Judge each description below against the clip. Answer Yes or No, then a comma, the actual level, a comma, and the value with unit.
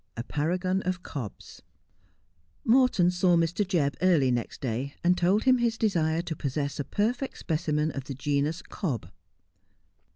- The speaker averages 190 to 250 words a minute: No, average, 150 wpm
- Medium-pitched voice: Yes, medium, 165 Hz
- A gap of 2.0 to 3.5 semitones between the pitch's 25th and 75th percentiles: No, average, 4.7 semitones